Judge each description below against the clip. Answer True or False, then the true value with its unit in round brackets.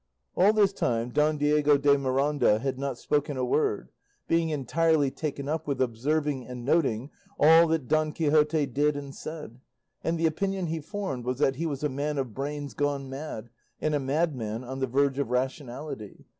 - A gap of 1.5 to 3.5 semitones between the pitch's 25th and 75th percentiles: True (2.8 semitones)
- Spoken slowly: False (185 wpm)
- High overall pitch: False (145 Hz)